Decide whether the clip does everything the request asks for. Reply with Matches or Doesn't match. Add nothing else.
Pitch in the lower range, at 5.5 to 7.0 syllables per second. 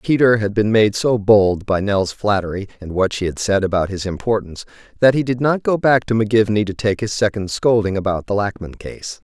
Matches